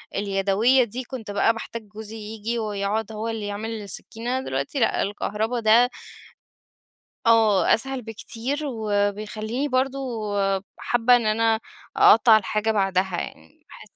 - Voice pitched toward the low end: No, high, 220 Hz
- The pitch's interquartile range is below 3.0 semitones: Yes, narrow, 2.4 semitones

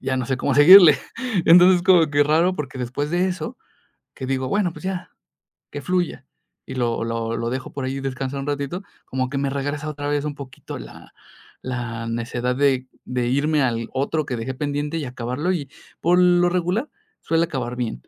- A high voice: No, medium, 140 Hz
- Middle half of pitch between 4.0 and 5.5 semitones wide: Yes, average, 4.4 semitones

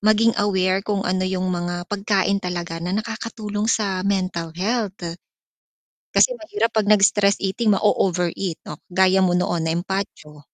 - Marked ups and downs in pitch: No, average, 2.7 semitones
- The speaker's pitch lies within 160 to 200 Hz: Yes, high, 190 Hz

